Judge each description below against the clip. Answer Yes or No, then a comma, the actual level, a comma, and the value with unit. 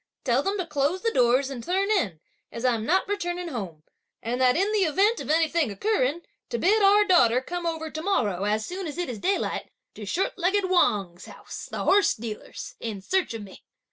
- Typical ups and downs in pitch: No, wide, 8.5 semitones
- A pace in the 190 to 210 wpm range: Yes, fast, 205 wpm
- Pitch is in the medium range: No, very high, 320 Hz